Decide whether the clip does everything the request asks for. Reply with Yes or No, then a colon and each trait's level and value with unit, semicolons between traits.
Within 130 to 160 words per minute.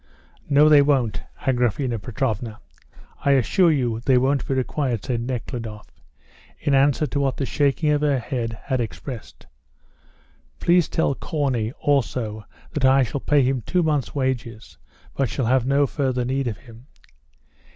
Yes: average, 150 wpm